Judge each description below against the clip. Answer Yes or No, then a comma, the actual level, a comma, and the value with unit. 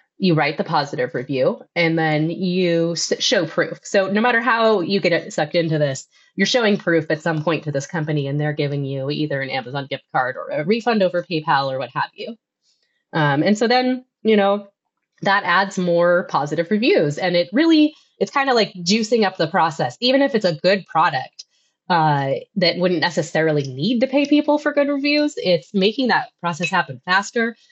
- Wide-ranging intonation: Yes, wide, 6.6 semitones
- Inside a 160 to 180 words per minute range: No, average, 200 wpm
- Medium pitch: Yes, medium, 180 Hz